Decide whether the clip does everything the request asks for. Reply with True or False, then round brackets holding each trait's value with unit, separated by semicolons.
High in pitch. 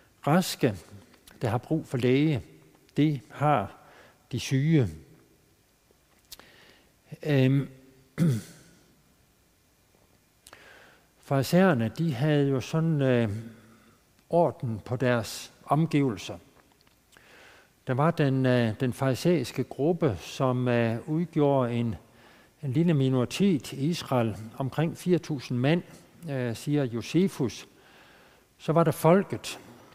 False (135 Hz)